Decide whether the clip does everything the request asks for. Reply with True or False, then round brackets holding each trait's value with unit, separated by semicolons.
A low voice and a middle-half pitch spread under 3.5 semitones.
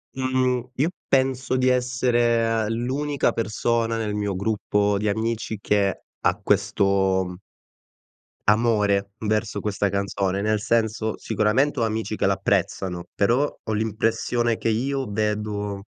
True (110 Hz; 2.7 semitones)